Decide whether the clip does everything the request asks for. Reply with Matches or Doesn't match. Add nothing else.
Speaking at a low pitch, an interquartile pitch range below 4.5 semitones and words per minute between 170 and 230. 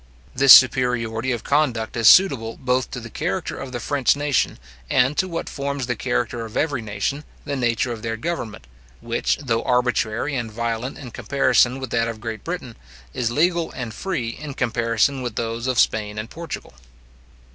Matches